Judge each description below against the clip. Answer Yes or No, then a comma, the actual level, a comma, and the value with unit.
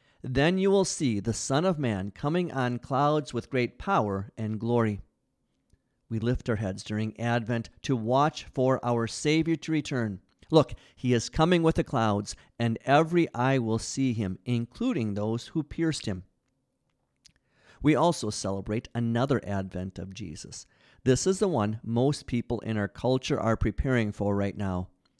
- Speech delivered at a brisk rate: No, average, 160 wpm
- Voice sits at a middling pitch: No, low, 120 Hz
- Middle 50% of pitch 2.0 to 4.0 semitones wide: No, average, 4.7 semitones